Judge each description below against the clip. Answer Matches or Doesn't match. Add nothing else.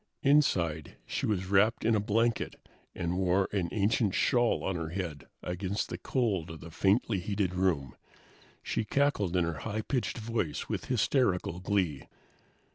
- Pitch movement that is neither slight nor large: Matches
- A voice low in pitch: Matches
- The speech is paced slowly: Doesn't match